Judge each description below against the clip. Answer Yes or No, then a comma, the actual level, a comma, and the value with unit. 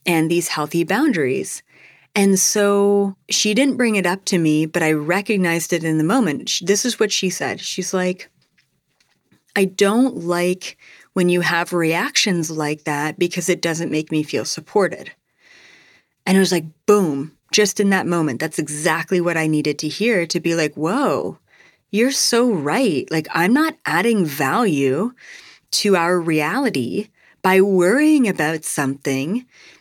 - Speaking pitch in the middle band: Yes, medium, 180 Hz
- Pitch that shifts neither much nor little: Yes, average, 4.3 semitones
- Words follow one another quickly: No, average, 155 wpm